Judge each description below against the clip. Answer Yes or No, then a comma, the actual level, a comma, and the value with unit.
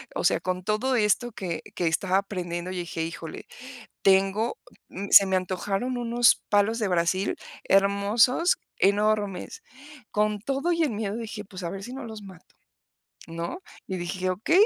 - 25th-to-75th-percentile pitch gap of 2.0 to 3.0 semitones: No, average, 3.4 semitones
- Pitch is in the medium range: No, high, 200 Hz